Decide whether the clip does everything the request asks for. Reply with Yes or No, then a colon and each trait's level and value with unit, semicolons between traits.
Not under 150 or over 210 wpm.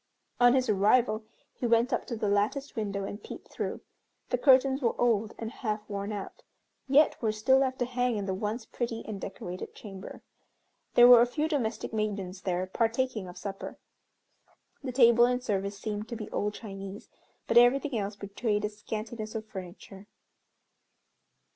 Yes: average, 170 wpm